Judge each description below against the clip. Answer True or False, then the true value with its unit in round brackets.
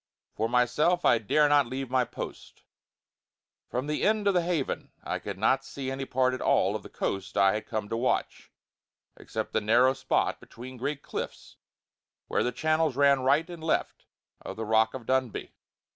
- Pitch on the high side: False (130 Hz)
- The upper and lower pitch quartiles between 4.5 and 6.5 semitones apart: False (4.1 semitones)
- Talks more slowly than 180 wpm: False (185 wpm)